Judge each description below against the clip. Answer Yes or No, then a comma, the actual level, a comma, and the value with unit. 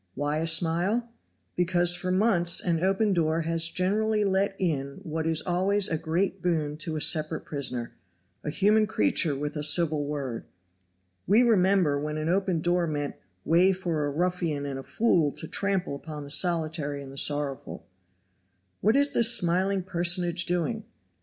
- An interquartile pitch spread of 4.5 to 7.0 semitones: No, average, 3.8 semitones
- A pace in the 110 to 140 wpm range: No, average, 160 wpm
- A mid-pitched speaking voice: Yes, medium, 170 Hz